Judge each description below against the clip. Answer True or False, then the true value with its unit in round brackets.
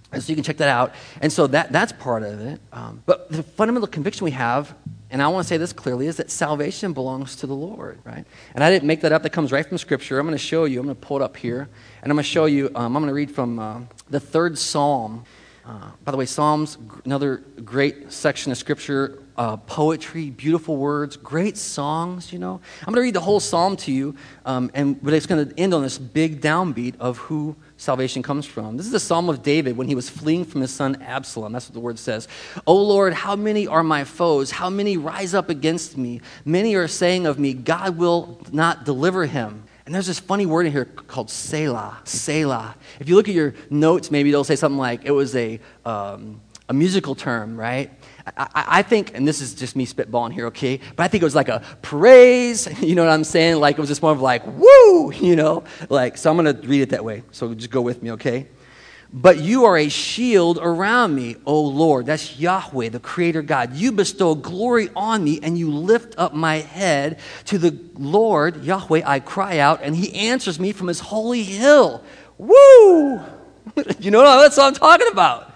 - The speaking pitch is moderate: True (150 Hz)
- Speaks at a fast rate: True (225 wpm)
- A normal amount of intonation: True (4.8 semitones)